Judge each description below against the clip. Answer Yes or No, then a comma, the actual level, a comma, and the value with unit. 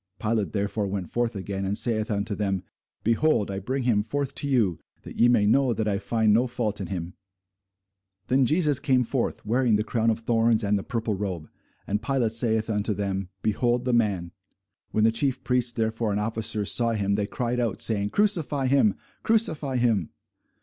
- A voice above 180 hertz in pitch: No, low, 110 Hz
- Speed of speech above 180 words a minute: Yes, average, 190 wpm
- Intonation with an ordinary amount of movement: Yes, average, 3.2 semitones